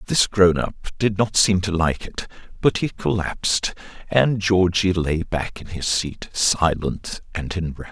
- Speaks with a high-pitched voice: No, very low, 95 Hz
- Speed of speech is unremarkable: Yes, average, 165 wpm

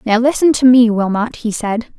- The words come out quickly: Yes, fast, 210 wpm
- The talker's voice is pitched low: No, high, 235 Hz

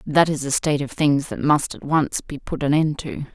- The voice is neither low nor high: Yes, medium, 145 Hz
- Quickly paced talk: Yes, fast, 270 wpm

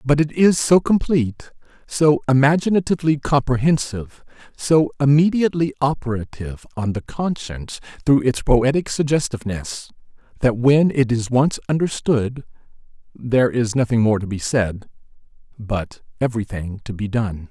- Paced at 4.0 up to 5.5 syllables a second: Yes, 5.0 syllables/s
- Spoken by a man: Yes, male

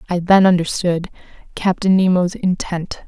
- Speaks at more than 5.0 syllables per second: No, 4.5 syllables/s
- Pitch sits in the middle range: Yes, medium, 180 Hz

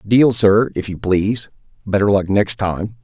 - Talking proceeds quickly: No, average, 180 wpm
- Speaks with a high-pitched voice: No, low, 105 Hz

